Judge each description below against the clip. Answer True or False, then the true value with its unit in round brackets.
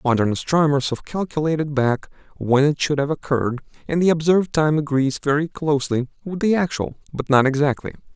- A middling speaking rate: True (170 wpm)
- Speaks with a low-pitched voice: False (145 Hz)